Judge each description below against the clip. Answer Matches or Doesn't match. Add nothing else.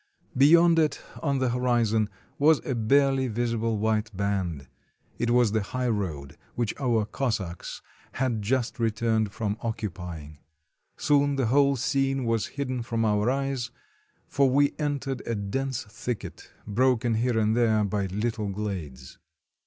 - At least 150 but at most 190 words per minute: Doesn't match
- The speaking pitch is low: Matches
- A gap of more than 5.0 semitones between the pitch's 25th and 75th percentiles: Doesn't match